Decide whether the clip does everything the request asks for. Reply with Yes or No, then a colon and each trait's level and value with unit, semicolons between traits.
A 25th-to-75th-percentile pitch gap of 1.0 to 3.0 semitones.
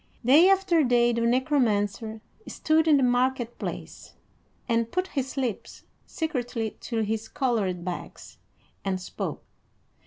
No: average, 4.0 semitones